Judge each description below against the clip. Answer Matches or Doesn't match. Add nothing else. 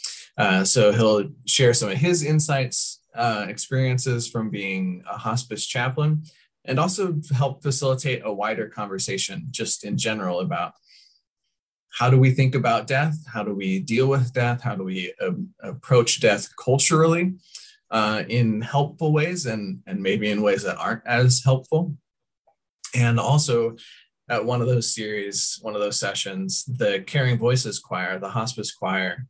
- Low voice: Matches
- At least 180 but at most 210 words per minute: Doesn't match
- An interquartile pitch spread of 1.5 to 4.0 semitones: Doesn't match